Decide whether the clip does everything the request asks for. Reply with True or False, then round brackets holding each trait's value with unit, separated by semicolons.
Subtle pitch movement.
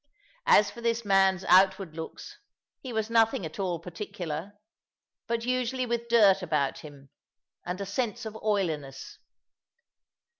False (5.1 semitones)